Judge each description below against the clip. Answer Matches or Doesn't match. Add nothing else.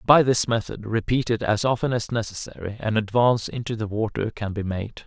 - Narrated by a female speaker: Doesn't match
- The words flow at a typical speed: Matches